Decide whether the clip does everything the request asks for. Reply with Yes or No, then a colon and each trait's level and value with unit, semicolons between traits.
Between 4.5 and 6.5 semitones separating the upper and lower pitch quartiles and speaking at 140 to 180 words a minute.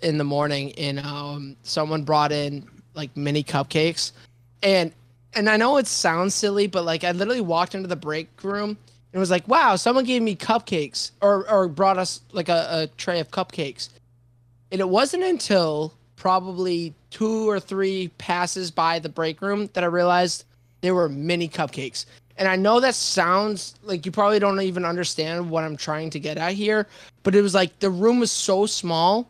No: average, 4.8 semitones; average, 190 wpm